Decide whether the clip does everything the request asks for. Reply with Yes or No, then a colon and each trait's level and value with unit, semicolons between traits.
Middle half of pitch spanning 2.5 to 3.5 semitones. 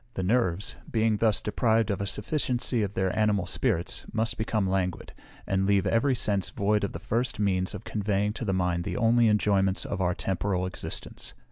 Yes: average, 2.8 semitones